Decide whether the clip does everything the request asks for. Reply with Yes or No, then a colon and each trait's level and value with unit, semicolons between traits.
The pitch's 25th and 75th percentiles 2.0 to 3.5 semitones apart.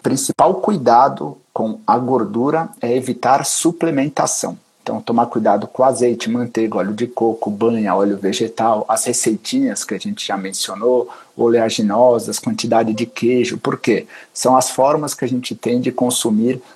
Yes: narrow, 2.4 semitones